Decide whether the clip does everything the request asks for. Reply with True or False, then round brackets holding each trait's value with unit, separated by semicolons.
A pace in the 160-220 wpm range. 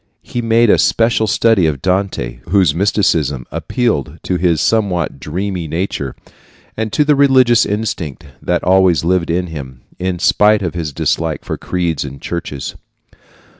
False (150 wpm)